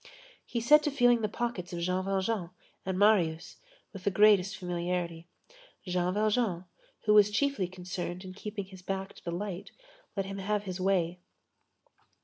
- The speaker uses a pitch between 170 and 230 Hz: Yes, high, 190 Hz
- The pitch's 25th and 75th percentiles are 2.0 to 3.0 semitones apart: Yes, average, 2.7 semitones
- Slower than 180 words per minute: Yes, average, 160 wpm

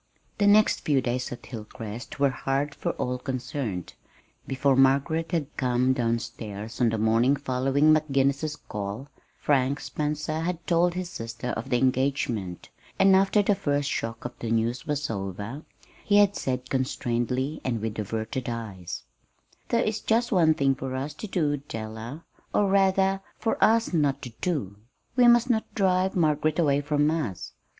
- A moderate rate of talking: Yes, average, 160 wpm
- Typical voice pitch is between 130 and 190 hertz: Yes, low, 135 Hz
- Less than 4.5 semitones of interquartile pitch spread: No, average, 5.2 semitones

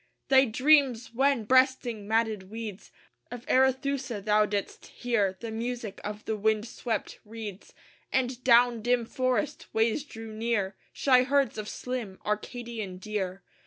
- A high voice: Yes, high, 230 Hz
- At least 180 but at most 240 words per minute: No, slow, 135 wpm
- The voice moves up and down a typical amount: Yes, average, 3.1 semitones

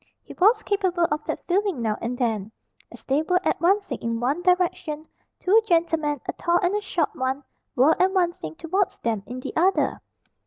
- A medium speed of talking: Yes, average, 180 wpm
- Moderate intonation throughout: No, wide, 6.1 semitones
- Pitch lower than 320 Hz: No, very high, 330 Hz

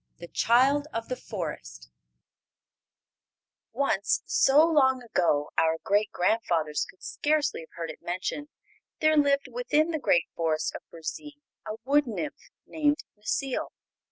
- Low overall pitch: No, high, 230 Hz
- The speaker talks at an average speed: No, slow, 130 wpm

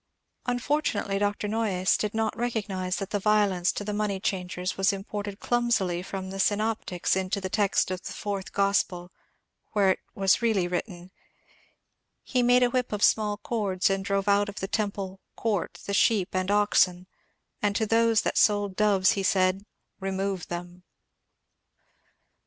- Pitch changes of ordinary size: No, narrow, 2.1 semitones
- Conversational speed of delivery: Yes, average, 160 wpm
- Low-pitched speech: No, high, 200 Hz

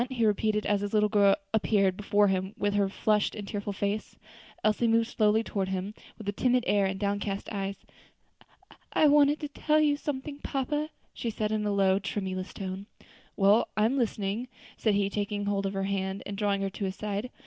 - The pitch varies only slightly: Yes, narrow, 2.1 semitones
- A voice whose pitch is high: Yes, high, 205 Hz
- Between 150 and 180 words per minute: No, average, 200 wpm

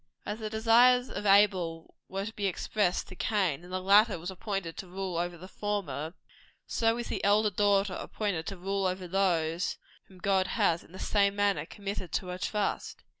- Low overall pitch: No, high, 195 Hz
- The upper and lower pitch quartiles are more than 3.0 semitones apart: No, narrow, 2.5 semitones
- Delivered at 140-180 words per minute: No, average, 190 wpm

